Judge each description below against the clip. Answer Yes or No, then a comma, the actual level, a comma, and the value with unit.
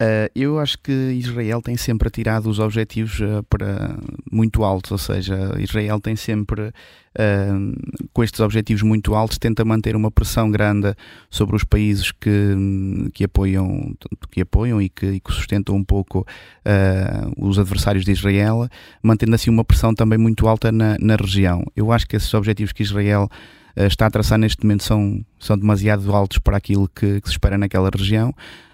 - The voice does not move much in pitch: Yes, narrow, 2.0 semitones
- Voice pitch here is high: No, low, 105 Hz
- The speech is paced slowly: No, average, 165 wpm